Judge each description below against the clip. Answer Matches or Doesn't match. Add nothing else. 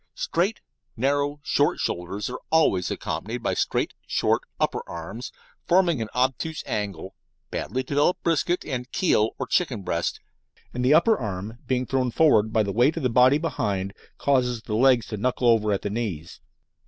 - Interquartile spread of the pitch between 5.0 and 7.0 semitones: Matches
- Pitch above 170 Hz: Doesn't match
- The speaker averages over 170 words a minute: Doesn't match